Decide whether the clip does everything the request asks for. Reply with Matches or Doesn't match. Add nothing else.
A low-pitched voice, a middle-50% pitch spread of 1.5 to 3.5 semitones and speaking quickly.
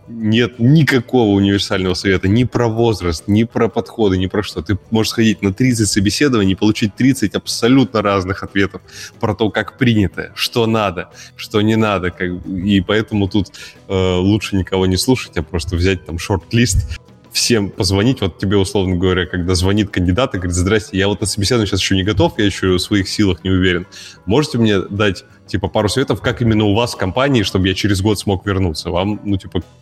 Matches